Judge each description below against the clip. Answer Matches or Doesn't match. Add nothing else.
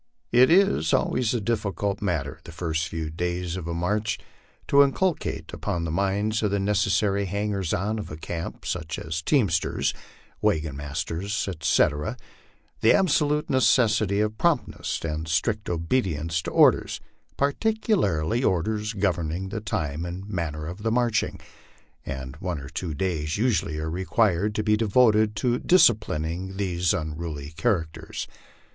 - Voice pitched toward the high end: Doesn't match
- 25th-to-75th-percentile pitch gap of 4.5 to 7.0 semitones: Matches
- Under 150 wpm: Matches